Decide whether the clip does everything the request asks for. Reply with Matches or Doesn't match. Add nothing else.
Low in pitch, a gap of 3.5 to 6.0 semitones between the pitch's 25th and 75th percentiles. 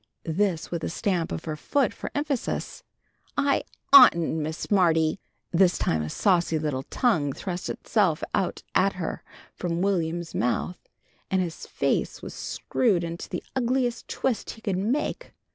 Doesn't match